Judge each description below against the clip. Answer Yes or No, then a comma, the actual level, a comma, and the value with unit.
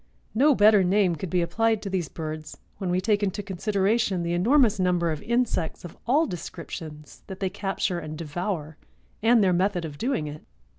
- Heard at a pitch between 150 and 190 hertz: Yes, medium, 185 Hz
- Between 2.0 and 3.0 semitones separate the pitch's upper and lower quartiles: No, average, 3.9 semitones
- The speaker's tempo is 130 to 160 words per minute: No, average, 185 wpm